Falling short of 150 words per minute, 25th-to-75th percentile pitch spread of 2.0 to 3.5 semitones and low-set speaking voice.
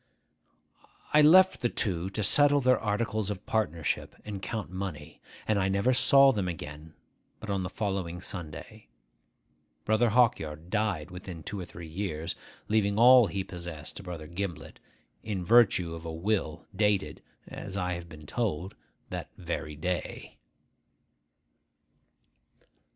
No: average, 140 wpm; average, 4.3 semitones; very low, 95 Hz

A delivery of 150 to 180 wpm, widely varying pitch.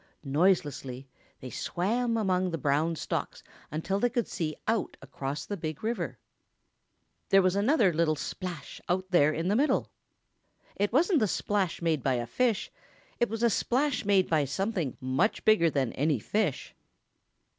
Yes: average, 155 wpm; wide, 6.5 semitones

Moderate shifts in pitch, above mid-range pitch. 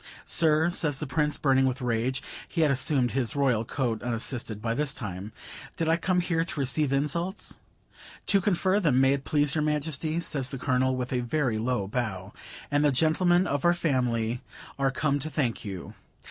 No: average, 4.1 semitones; medium, 140 Hz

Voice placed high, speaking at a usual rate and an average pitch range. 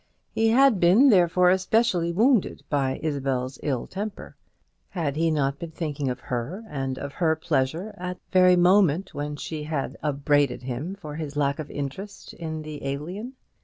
No: medium, 160 Hz; average, 165 wpm; average, 4.6 semitones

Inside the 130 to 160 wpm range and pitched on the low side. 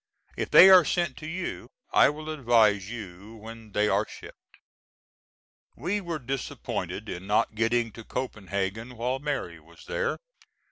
Yes: average, 145 wpm; low, 115 Hz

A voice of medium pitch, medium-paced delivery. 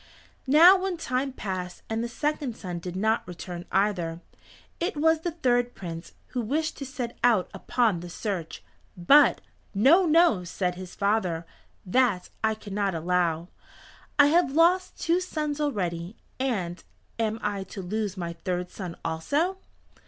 No: high, 215 Hz; average, 150 wpm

